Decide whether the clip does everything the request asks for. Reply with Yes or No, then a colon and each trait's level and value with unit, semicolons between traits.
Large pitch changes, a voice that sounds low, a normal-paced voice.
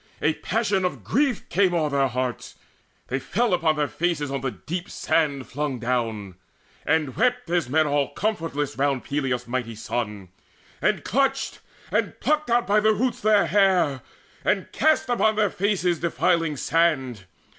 No: wide, 7.2 semitones; medium, 160 Hz; average, 155 wpm